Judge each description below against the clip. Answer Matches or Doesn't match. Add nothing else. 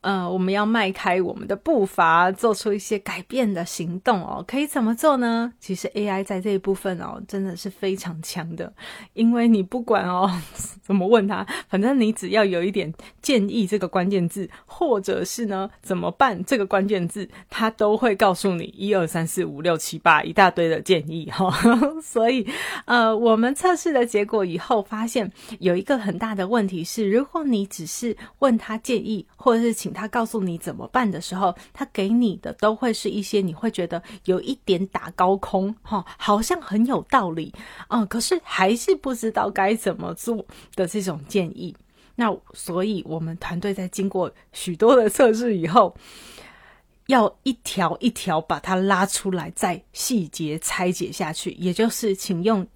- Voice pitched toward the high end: Matches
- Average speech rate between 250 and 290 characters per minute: Matches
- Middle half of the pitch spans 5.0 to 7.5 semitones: Doesn't match